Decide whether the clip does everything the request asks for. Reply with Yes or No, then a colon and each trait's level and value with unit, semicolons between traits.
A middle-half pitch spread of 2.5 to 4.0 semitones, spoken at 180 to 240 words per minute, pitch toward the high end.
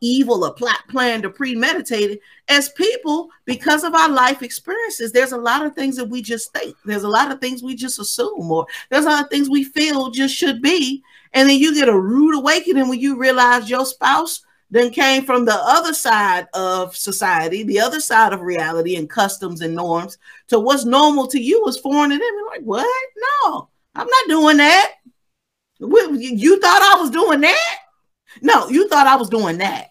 No: average, 4.8 semitones; average, 200 wpm; very high, 270 Hz